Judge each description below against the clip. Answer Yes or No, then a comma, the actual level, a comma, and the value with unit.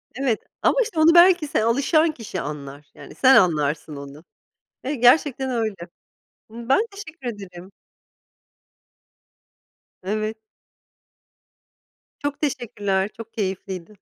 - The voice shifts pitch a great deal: Yes, wide, 7.1 semitones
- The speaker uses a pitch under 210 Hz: No, high, 225 Hz